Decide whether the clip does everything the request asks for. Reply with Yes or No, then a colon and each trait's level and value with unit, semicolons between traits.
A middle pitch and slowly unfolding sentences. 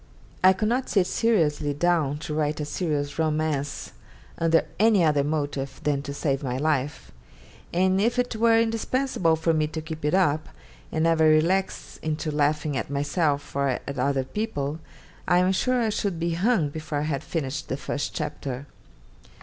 No: medium, 155 Hz; average, 175 wpm